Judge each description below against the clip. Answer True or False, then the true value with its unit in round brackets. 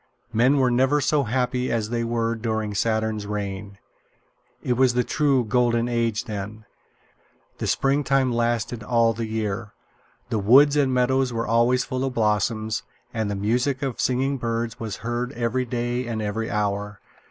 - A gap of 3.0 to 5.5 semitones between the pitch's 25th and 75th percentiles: False (2.5 semitones)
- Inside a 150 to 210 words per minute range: True (160 wpm)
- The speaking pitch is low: True (115 Hz)